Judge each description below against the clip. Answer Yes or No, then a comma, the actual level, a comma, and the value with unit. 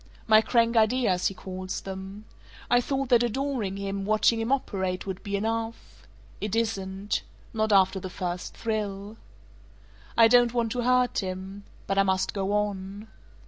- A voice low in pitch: No, high, 210 Hz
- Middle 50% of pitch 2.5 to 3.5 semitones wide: Yes, average, 3.1 semitones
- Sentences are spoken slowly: No, average, 155 wpm